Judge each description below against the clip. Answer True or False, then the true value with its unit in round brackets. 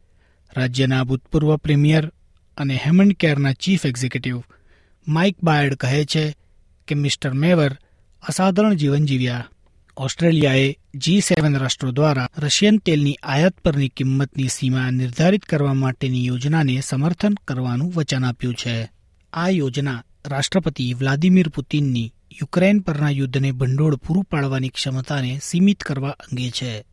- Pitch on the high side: False (140 Hz)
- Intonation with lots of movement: False (3.6 semitones)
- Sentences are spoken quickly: False (120 wpm)